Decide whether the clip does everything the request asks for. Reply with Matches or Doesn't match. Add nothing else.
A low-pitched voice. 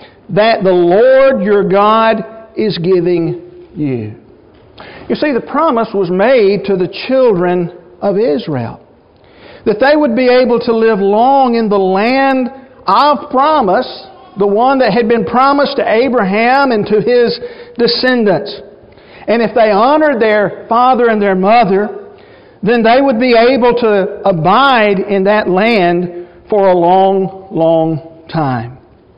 Doesn't match